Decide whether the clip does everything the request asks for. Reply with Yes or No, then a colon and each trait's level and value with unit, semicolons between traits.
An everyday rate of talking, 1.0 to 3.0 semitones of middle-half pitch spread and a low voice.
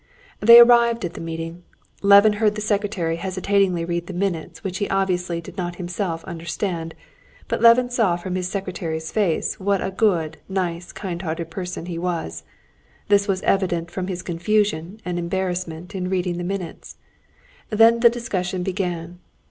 No: average, 160 wpm; average, 2.7 semitones; medium, 185 Hz